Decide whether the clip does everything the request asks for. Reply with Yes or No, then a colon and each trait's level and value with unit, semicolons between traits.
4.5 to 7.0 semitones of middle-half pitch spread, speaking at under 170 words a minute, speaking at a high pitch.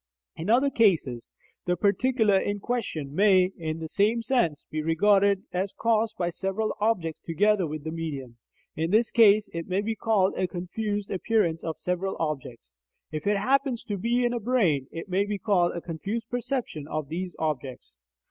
No: average, 5.1 semitones; average, 175 wpm; high, 195 Hz